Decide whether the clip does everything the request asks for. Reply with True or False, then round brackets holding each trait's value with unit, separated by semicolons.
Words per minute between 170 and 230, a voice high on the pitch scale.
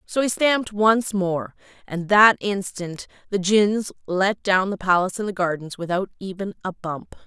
True (175 wpm; 195 Hz)